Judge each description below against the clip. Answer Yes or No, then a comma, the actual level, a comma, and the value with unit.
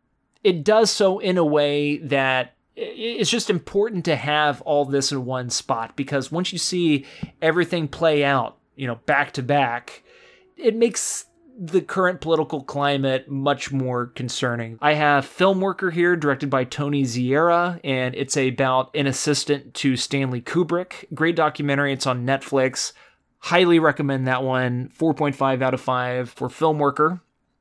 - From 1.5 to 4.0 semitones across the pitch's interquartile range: No, average, 4.5 semitones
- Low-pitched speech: No, medium, 145 Hz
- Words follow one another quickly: No, average, 150 wpm